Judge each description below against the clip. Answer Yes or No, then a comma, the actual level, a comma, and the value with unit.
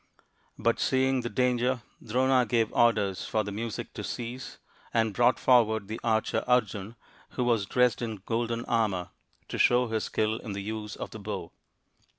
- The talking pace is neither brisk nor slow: Yes, average, 165 wpm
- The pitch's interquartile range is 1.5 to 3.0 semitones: Yes, narrow, 2.4 semitones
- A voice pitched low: Yes, low, 115 Hz